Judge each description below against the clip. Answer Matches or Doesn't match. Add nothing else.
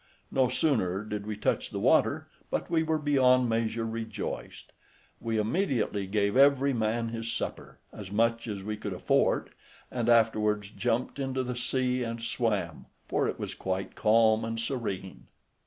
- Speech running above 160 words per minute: Doesn't match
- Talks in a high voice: Doesn't match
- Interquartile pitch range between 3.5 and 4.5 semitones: Doesn't match